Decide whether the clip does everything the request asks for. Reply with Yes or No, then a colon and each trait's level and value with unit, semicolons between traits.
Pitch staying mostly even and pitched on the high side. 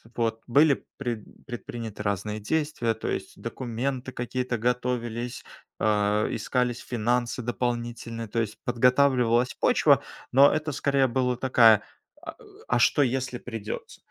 No: narrow, 1.9 semitones; low, 120 Hz